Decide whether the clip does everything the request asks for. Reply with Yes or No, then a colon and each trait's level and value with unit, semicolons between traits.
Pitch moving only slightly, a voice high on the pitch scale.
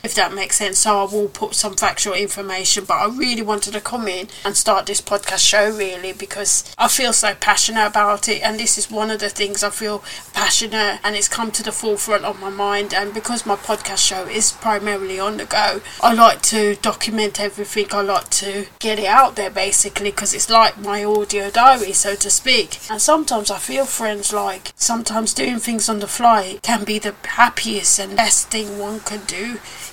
Yes: narrow, 1.5 semitones; high, 210 Hz